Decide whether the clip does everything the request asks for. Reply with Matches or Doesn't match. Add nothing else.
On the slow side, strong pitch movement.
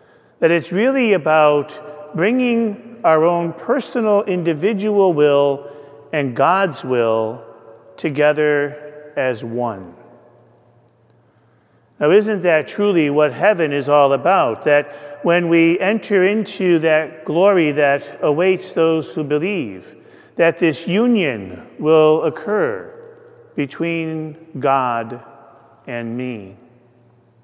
Matches